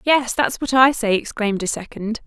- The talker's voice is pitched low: No, high, 235 Hz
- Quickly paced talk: Yes, fast, 210 wpm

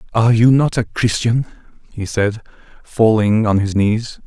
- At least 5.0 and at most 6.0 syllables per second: No, 4.6 syllables/s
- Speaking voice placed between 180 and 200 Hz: No, low, 110 Hz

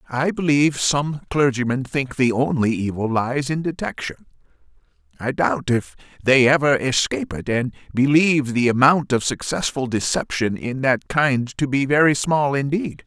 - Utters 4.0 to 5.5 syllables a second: Yes, 4.6 syllables/s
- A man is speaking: Yes, male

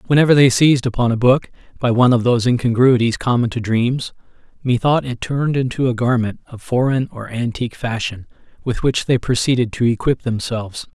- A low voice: Yes, low, 125 Hz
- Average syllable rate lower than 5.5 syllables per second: No, 5.8 syllables/s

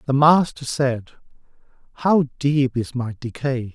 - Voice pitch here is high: No, low, 135 Hz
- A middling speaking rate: No, slow, 130 wpm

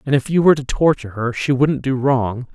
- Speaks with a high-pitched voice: No, low, 135 Hz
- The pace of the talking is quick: Yes, fast, 260 wpm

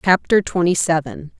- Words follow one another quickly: No, slow, 130 wpm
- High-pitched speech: No, medium, 175 Hz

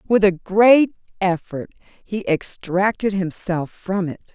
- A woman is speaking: Yes, female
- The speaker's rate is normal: No, slow, 125 wpm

